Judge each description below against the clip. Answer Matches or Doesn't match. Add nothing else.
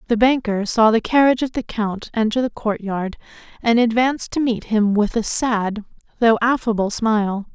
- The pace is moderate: Matches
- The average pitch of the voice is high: Matches